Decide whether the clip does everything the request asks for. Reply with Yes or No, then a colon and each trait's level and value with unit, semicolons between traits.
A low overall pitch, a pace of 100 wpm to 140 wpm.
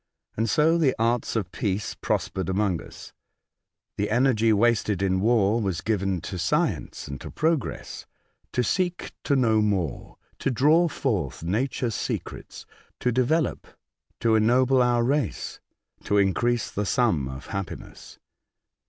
Yes: low, 110 Hz; slow, 135 wpm